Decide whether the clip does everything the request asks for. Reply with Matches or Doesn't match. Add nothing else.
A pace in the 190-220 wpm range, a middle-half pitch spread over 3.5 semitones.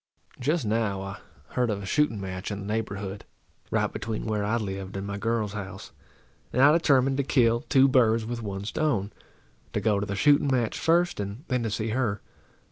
Matches